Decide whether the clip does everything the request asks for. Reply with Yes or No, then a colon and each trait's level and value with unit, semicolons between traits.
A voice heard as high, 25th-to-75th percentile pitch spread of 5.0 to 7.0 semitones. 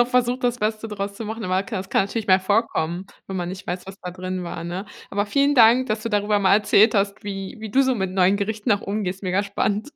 No: high, 205 Hz; average, 2.8 semitones